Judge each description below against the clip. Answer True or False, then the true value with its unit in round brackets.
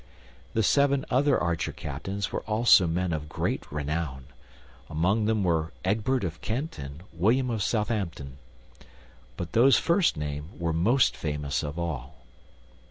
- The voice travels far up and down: True (6.6 semitones)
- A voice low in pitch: True (90 Hz)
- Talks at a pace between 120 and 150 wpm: True (140 wpm)